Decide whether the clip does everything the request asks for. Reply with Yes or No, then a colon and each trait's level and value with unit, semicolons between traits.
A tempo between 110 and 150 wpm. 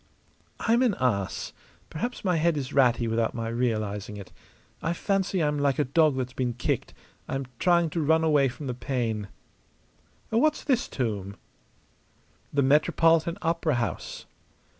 Yes: average, 145 wpm